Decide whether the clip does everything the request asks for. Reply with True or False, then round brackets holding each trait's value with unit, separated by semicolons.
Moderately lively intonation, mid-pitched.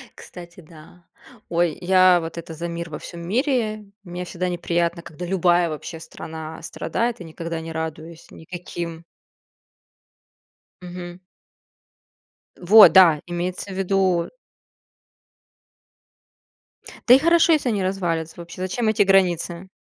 False (2.1 semitones; 175 Hz)